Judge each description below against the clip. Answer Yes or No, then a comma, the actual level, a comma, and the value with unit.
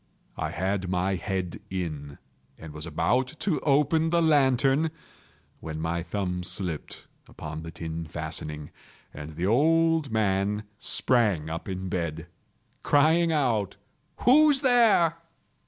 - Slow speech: Yes, slow, 120 wpm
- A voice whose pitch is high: No, low, 100 Hz